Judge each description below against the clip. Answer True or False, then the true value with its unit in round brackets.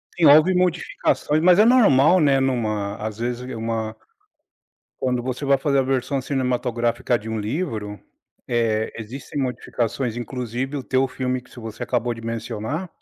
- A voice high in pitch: False (125 Hz)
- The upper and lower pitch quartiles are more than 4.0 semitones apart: False (3.4 semitones)